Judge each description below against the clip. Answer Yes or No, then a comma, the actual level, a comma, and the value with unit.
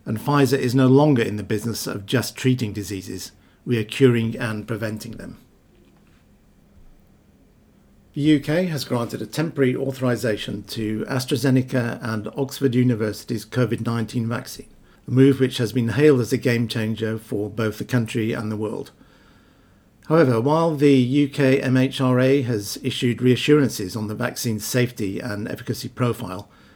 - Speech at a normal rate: Yes, average, 145 wpm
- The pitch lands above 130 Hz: No, low, 120 Hz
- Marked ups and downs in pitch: No, average, 3.3 semitones